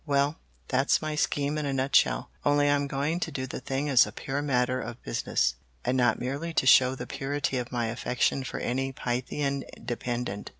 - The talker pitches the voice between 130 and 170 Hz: Yes, low, 135 Hz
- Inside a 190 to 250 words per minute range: Yes, average, 200 wpm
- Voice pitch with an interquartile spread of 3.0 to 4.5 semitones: No, narrow, 2.5 semitones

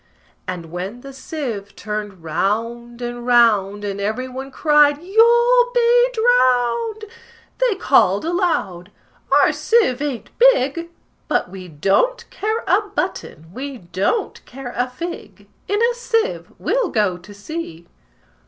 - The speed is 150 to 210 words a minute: No, slow, 135 wpm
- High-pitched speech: Yes, very high, 255 Hz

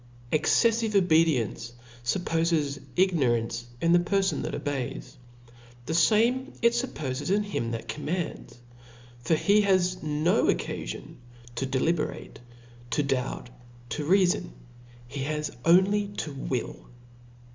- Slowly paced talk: Yes, slow, 105 wpm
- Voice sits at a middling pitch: Yes, medium, 155 Hz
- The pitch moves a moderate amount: No, wide, 6.3 semitones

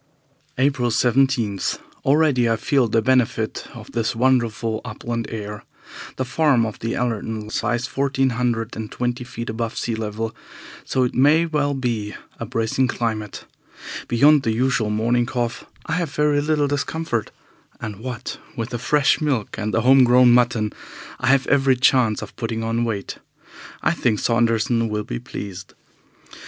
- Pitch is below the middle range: Yes, low, 120 Hz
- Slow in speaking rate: No, average, 155 wpm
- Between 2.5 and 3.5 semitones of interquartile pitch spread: Yes, average, 2.9 semitones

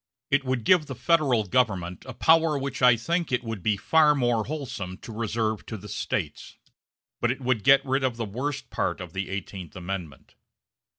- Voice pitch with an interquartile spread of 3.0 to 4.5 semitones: No, average, 5.3 semitones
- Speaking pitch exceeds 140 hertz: No, low, 120 Hz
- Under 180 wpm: No, average, 190 wpm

